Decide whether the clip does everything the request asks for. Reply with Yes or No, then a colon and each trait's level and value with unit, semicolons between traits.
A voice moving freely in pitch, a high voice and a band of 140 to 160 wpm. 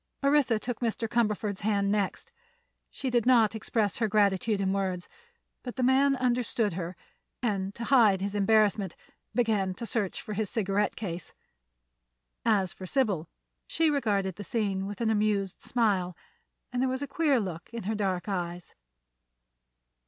No: average, 3.5 semitones; high, 210 Hz; average, 155 wpm